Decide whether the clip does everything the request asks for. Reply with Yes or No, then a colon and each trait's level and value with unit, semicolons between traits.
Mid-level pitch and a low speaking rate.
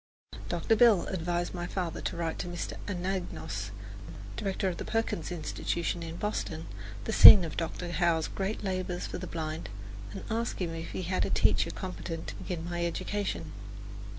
No: medium, 175 Hz; average, 170 wpm